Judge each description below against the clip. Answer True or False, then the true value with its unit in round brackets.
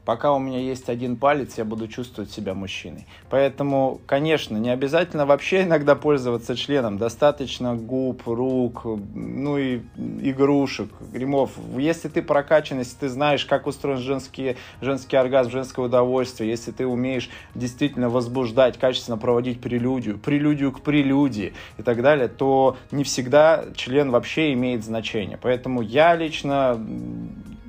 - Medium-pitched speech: False (130 Hz)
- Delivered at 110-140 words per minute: True (135 wpm)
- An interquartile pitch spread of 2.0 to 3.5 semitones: True (2.9 semitones)